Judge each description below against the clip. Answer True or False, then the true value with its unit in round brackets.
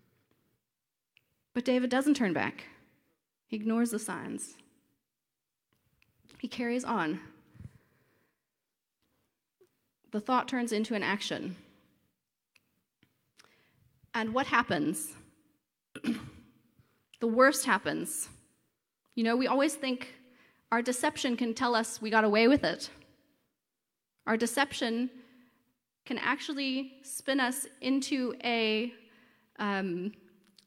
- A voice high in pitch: True (245 Hz)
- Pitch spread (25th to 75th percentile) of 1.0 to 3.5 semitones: True (2.7 semitones)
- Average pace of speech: False (95 wpm)